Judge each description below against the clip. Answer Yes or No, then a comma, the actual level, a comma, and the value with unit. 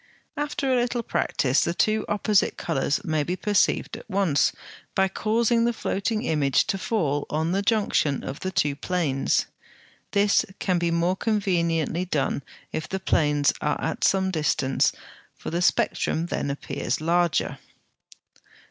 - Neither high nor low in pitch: Yes, medium, 175 Hz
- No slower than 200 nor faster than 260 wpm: No, average, 150 wpm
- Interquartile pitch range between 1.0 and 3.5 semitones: No, average, 5.1 semitones